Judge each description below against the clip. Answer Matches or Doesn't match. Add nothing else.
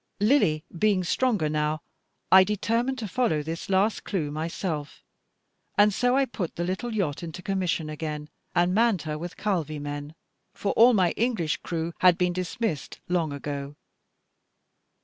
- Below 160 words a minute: Matches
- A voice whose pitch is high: Doesn't match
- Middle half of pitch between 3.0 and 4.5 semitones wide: Doesn't match